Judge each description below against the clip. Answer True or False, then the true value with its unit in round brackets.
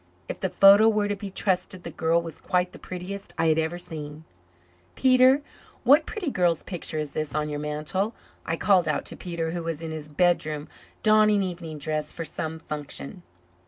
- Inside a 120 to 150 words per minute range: False (190 wpm)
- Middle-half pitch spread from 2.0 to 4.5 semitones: True (4.2 semitones)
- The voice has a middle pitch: True (170 Hz)